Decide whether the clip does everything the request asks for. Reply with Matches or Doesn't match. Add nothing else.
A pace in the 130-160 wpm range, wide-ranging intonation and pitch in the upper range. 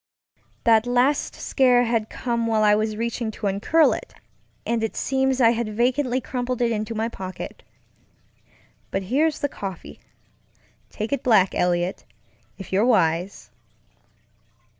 Doesn't match